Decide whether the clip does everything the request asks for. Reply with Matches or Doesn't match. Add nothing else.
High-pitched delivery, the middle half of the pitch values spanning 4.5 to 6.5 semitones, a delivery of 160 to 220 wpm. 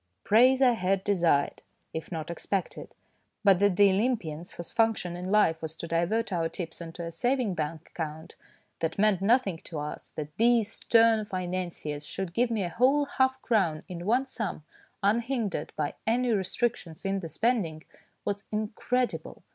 Matches